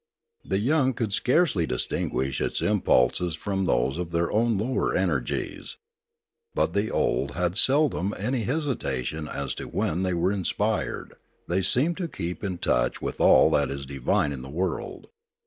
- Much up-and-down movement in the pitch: Yes, wide, 7.6 semitones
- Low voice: Yes, very low, 95 Hz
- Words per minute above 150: Yes, average, 160 wpm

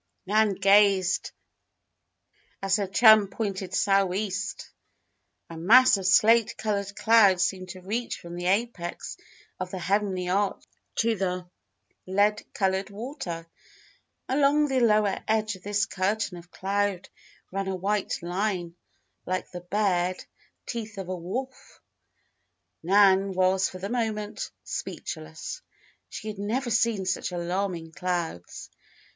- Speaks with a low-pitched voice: No, high, 195 Hz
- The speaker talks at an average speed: No, slow, 125 wpm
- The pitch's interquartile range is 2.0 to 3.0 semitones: Yes, narrow, 2.5 semitones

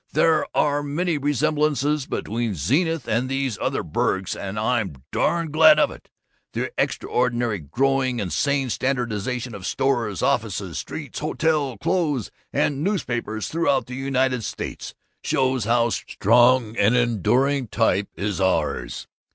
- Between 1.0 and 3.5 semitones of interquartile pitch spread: No, average, 4.7 semitones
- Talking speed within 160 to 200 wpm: No, slow, 135 wpm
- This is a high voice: No, low, 125 Hz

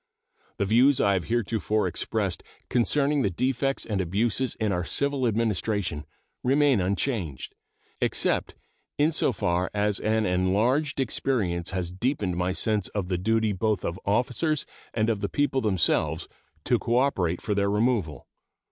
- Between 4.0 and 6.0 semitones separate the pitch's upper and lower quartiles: Yes, average, 5.2 semitones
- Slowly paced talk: No, average, 145 wpm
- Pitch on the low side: Yes, low, 110 Hz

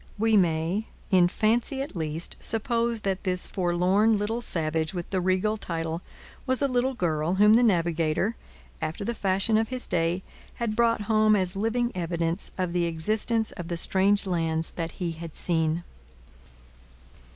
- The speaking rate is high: No, average, 160 wpm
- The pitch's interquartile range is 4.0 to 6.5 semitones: Yes, average, 4.6 semitones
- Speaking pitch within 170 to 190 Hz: Yes, medium, 185 Hz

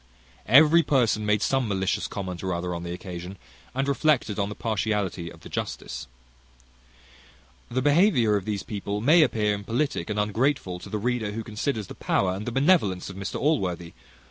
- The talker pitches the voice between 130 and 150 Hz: No, low, 105 Hz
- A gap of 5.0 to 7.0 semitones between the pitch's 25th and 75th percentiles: Yes, average, 5.3 semitones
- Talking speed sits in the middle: Yes, average, 170 wpm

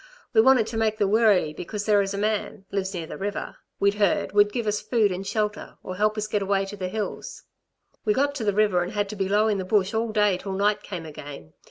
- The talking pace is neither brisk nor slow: No, fast, 260 wpm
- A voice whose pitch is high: Yes, high, 205 Hz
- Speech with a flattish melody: Yes, narrow, 1.7 semitones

